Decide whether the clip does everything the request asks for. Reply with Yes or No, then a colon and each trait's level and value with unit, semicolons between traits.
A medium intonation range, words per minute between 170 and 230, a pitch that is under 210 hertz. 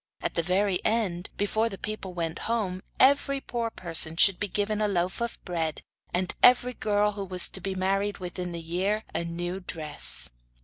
Yes: average, 3.3 semitones; average, 185 wpm; high, 190 Hz